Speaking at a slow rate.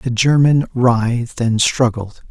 Yes: slow, 130 wpm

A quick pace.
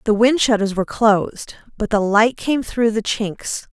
No: average, 190 wpm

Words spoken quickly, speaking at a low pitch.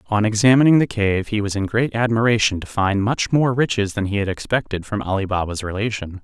Yes: fast, 210 wpm; low, 110 Hz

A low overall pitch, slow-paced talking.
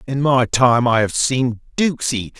No: low, 125 Hz; average, 200 wpm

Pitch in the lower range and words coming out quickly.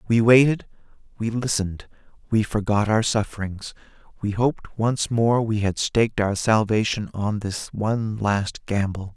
No: low, 110 Hz; average, 145 wpm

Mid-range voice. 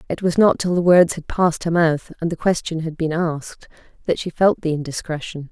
Yes: medium, 165 Hz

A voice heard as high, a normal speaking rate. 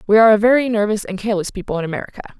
No: high, 210 Hz; fast, 250 wpm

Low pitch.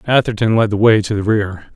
Yes: low, 105 Hz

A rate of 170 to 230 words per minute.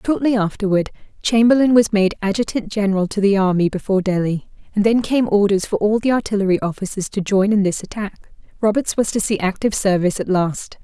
Yes: average, 190 wpm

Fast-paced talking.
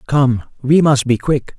No: average, 190 wpm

